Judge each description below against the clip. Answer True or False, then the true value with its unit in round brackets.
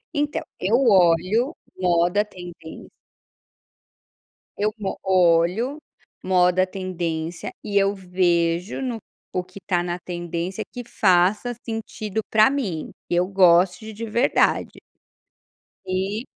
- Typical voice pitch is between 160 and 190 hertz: True (185 Hz)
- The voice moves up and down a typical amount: True (3.5 semitones)